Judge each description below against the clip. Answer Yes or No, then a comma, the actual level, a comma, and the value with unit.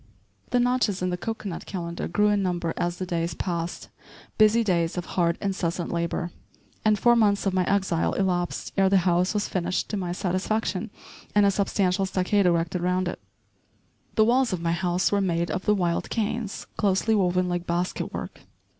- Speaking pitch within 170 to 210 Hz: Yes, medium, 185 Hz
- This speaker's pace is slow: No, average, 185 wpm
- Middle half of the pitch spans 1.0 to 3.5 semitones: Yes, average, 2.7 semitones